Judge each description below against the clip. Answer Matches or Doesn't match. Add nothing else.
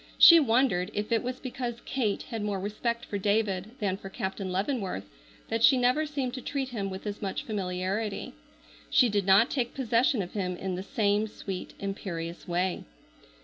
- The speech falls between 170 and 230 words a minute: Matches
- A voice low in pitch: Doesn't match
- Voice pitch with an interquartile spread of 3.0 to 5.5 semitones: Matches